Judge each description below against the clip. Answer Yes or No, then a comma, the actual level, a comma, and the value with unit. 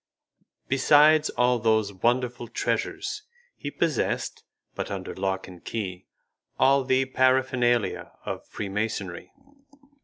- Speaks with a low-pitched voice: Yes, low, 120 Hz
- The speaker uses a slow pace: Yes, slow, 100 wpm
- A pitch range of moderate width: Yes, average, 4.3 semitones